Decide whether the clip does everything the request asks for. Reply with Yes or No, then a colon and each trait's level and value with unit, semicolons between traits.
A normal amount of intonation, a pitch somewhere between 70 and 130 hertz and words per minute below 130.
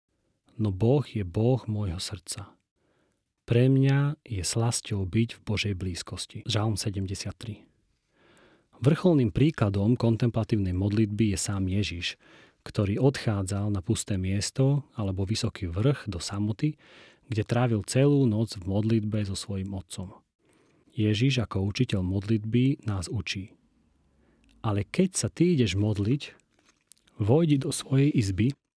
Yes: average, 4.1 semitones; low, 110 Hz; average, 120 wpm